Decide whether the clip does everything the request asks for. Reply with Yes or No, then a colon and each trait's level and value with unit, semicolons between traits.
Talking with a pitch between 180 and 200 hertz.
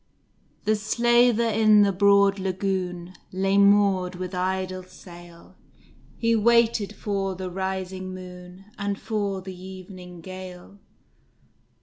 Yes: high, 190 Hz